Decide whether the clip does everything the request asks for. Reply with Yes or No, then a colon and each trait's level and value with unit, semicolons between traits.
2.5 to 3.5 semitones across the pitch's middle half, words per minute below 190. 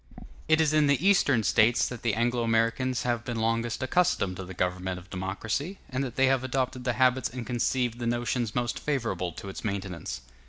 No: average, 3.1 semitones; average, 200 wpm